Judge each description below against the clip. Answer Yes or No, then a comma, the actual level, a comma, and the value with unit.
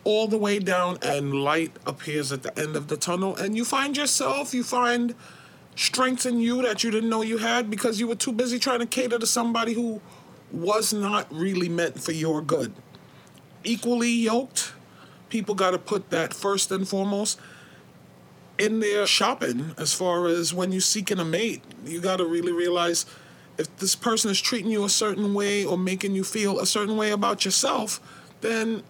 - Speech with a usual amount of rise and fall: Yes, average, 4.7 semitones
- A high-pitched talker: Yes, high, 205 Hz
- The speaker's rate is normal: Yes, average, 185 wpm